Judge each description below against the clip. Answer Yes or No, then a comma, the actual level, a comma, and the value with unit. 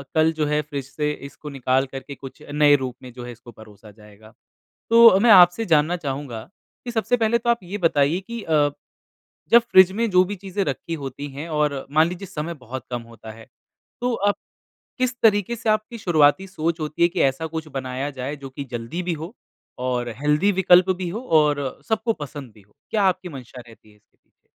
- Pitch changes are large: Yes, wide, 6.5 semitones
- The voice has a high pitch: No, medium, 150 Hz